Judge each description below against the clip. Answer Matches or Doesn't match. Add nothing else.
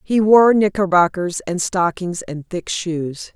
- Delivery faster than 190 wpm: Doesn't match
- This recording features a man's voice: Doesn't match